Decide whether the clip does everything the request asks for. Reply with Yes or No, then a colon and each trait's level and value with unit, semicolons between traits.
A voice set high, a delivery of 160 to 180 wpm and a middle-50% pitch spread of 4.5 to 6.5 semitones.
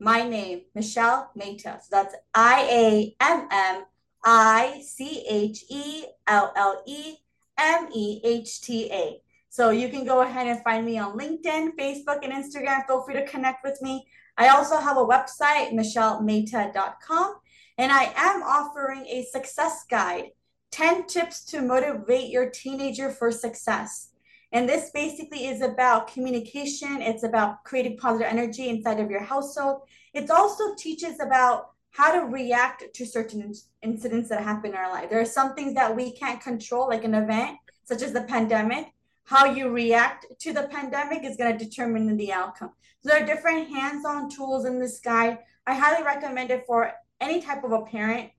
No: very high, 255 Hz; average, 175 wpm; average, 3.8 semitones